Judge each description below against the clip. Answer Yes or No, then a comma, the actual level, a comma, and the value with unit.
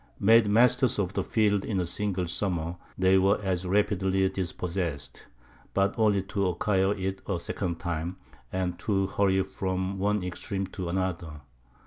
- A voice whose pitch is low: Yes, very low, 95 Hz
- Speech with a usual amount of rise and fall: No, narrow, 2.0 semitones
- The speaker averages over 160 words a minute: No, average, 150 wpm